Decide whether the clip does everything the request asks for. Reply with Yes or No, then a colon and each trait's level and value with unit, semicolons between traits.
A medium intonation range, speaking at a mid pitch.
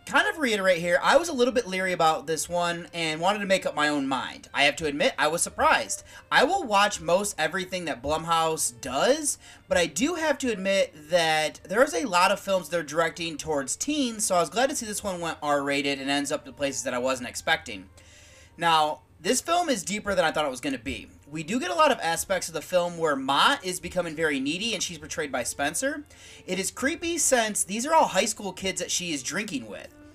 No: wide, 6.9 semitones; medium, 180 Hz